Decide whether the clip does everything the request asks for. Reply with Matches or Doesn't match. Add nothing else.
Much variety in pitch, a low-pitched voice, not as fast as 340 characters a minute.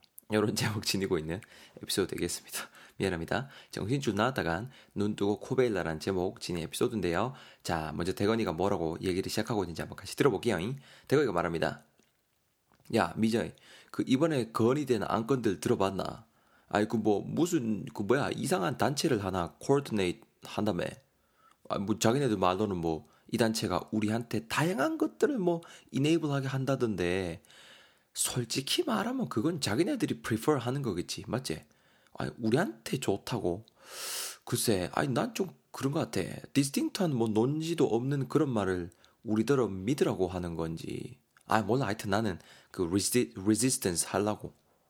Doesn't match